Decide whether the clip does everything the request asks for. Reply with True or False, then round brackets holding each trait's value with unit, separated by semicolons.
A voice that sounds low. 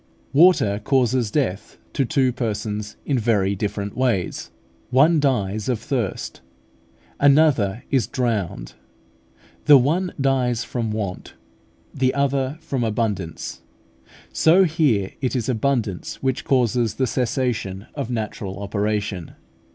True (120 Hz)